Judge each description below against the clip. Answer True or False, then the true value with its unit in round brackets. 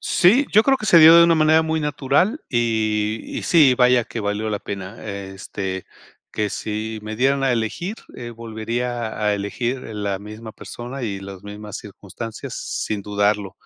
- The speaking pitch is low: True (110 Hz)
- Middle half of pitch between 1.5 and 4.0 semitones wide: False (4.7 semitones)